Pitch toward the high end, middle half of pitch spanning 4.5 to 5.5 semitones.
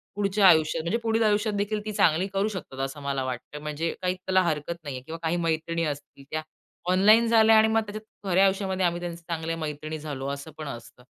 No: medium, 170 Hz; average, 4.9 semitones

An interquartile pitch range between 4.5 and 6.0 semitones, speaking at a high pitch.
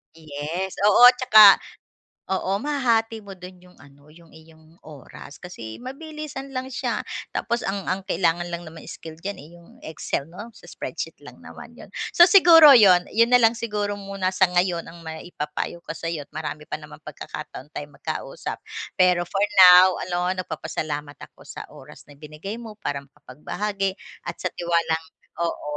No: average, 5.0 semitones; medium, 180 Hz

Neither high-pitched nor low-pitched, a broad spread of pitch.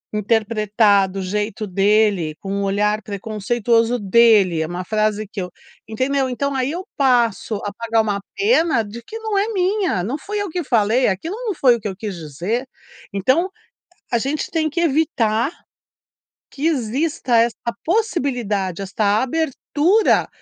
No: high, 230 Hz; wide, 5.8 semitones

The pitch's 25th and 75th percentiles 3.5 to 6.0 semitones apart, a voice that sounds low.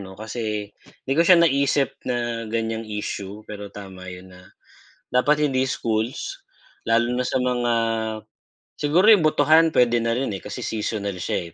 Yes: average, 4.5 semitones; low, 115 Hz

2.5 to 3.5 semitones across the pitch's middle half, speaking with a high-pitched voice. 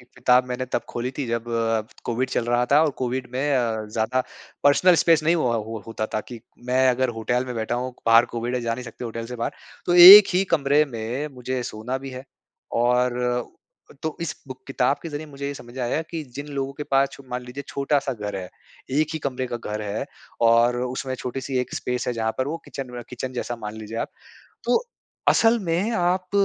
No: average, 2.9 semitones; low, 125 Hz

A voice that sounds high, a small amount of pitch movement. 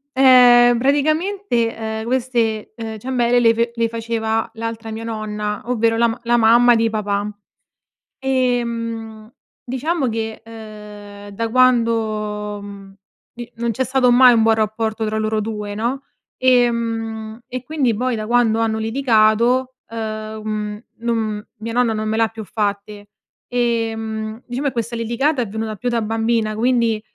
Yes: high, 225 Hz; narrow, 2.0 semitones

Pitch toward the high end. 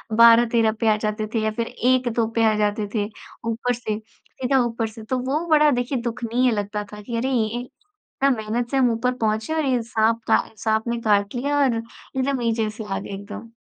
Yes: high, 230 Hz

